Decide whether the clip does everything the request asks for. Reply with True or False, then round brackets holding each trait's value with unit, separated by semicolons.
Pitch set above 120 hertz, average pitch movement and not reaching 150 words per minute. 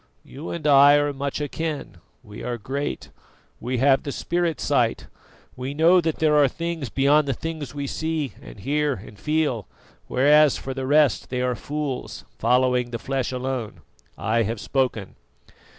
False (140 Hz; 3.1 semitones; 165 wpm)